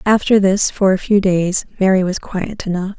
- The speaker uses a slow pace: No, average, 200 wpm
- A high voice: Yes, high, 195 Hz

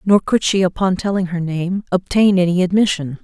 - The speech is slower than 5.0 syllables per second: No, 5.2 syllables/s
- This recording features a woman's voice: Yes, female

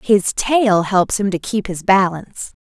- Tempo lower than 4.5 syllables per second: Yes, 4.0 syllables/s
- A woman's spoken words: Yes, female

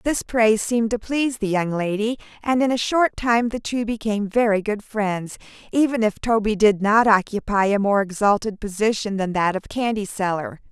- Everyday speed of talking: Yes, average, 190 wpm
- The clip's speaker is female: Yes, female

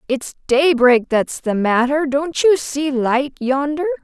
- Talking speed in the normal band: Yes, average, 150 wpm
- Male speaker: No, female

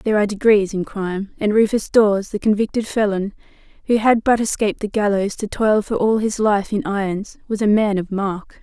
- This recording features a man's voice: No, female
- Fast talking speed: Yes, fast, 210 wpm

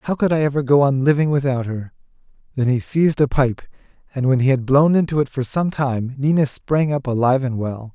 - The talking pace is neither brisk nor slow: No, fast, 225 wpm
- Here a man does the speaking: Yes, male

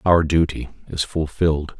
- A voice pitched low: Yes, very low, 80 Hz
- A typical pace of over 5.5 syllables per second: No, 4.6 syllables/s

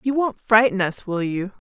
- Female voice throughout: Yes, female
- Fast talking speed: Yes, fast, 215 wpm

